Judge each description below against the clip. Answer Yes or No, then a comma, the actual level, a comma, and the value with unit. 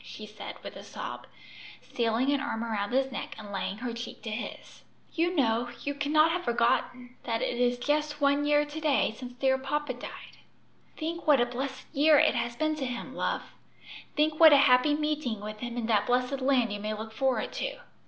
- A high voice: Yes, very high, 260 Hz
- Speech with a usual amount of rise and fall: Yes, average, 3.9 semitones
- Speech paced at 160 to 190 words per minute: No, fast, 205 wpm